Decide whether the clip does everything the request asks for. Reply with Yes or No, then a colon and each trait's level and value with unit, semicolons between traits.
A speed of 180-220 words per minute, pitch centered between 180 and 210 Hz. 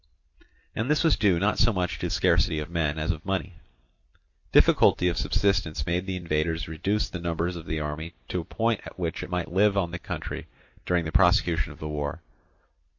No: average, 200 wpm; very low, 85 Hz